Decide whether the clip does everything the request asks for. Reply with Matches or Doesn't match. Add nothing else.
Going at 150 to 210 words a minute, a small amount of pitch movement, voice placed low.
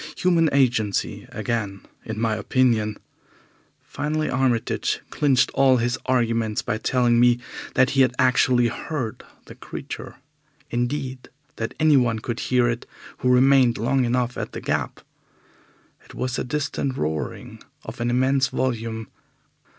Doesn't match